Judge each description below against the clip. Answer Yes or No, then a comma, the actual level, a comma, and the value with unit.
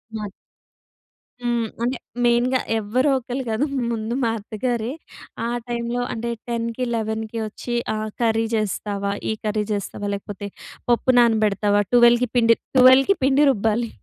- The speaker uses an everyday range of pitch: No, narrow, 2.1 semitones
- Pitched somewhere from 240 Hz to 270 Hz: No, high, 230 Hz